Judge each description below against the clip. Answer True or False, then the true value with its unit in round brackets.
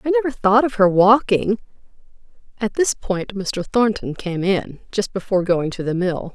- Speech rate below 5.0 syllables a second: True (4.7 syllables/s)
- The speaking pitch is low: False (205 Hz)